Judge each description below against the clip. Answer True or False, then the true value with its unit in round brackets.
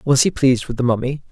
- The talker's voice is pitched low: True (130 Hz)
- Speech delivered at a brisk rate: True (275 wpm)